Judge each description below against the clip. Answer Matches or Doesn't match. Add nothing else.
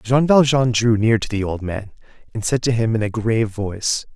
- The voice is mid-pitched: Doesn't match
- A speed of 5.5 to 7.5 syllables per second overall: Doesn't match